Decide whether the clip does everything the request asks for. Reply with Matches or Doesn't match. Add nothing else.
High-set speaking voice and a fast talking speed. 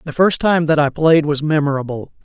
Doesn't match